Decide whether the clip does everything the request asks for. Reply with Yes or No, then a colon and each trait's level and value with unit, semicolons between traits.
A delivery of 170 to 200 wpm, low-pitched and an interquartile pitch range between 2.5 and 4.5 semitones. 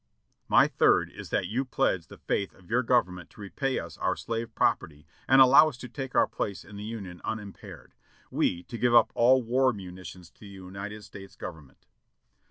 No: average, 195 wpm; low, 105 Hz; average, 5.0 semitones